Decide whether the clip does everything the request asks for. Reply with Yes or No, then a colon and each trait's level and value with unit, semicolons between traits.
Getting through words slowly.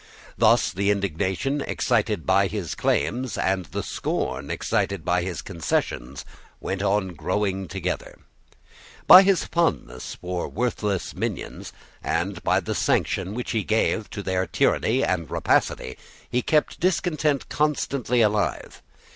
Yes: slow, 130 wpm